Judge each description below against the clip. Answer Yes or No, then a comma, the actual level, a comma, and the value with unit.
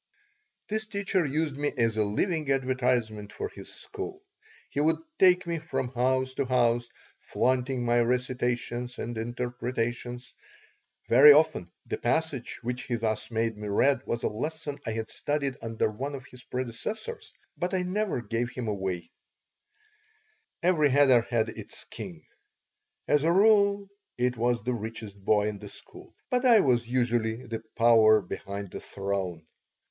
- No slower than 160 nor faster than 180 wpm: No, average, 150 wpm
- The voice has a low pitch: Yes, low, 125 Hz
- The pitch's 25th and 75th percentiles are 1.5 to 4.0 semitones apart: No, average, 4.6 semitones